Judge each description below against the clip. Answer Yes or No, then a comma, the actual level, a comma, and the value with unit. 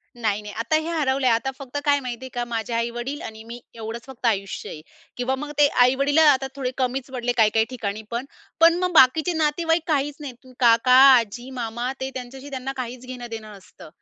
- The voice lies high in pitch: Yes, very high, 255 Hz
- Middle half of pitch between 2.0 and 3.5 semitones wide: Yes, average, 3.0 semitones